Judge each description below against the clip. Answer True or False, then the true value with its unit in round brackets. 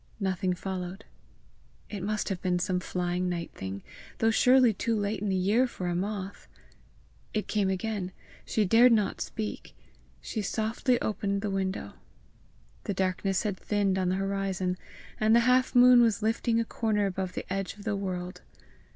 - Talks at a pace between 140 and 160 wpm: False (170 wpm)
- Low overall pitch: False (200 Hz)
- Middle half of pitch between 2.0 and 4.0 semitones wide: True (2.9 semitones)